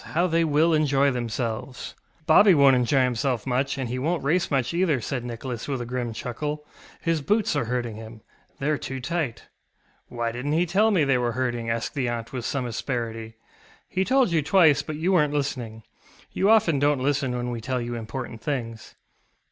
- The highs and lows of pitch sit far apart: No, average, 4.3 semitones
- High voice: No, low, 135 Hz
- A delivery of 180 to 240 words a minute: Yes, average, 190 wpm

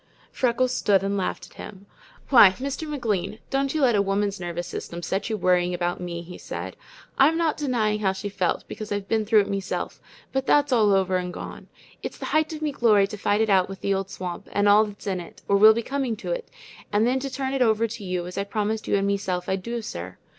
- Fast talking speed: Yes, fast, 245 wpm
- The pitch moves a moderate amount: Yes, average, 4.0 semitones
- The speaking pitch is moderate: No, high, 205 Hz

